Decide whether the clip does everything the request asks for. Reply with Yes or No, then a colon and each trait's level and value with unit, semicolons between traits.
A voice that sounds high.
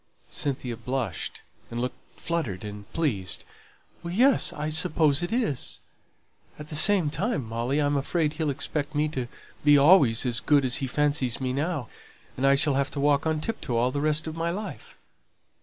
No: medium, 145 Hz